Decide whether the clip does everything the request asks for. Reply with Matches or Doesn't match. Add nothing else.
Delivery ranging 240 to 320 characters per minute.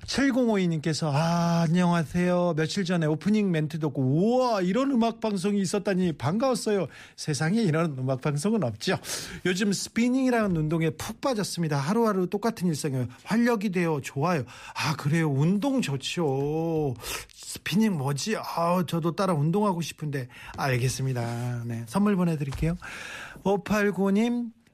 Matches